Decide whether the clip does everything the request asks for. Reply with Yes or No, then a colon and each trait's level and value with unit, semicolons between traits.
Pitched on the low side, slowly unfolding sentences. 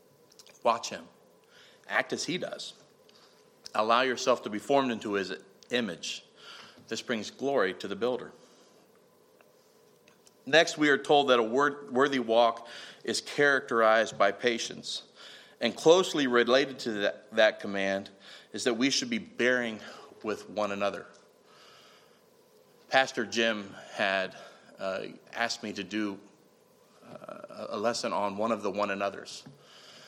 Yes: low, 125 Hz; slow, 130 wpm